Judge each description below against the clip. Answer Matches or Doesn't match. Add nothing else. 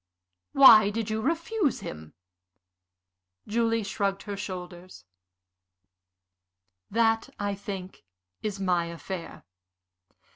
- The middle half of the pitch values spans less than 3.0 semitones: Doesn't match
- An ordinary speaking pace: Doesn't match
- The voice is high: Matches